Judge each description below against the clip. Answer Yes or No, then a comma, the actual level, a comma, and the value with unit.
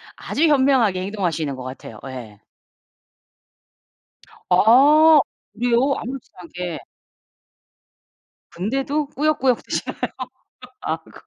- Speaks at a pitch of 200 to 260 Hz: Yes, high, 230 Hz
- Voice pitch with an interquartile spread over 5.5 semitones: Yes, wide, 8.5 semitones